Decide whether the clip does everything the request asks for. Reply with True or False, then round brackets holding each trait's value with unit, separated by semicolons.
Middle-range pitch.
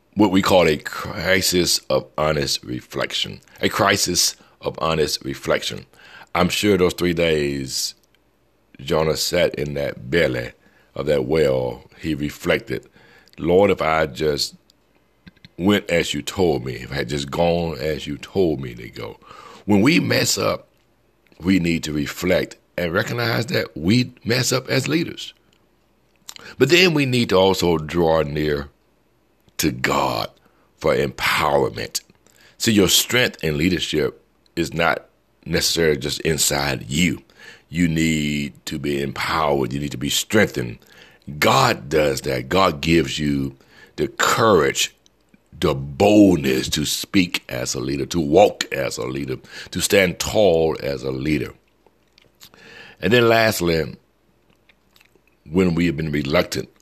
False (80 Hz)